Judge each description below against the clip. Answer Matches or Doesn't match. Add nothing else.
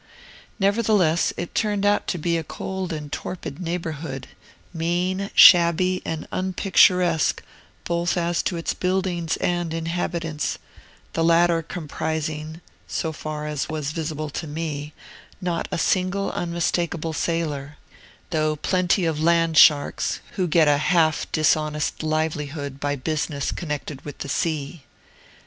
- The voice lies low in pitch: Doesn't match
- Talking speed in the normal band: Doesn't match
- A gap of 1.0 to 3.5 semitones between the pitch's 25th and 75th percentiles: Matches